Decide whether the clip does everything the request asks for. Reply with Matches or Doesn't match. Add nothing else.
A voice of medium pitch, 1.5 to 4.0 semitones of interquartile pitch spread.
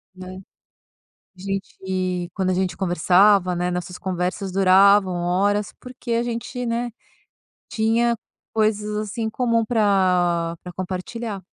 Doesn't match